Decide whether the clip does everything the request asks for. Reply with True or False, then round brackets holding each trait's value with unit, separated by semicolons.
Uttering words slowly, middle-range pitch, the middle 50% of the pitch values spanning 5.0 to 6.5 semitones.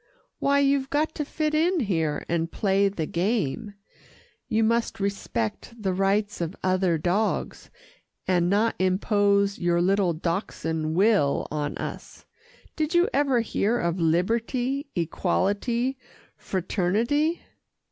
False (120 wpm; 200 Hz; 5.5 semitones)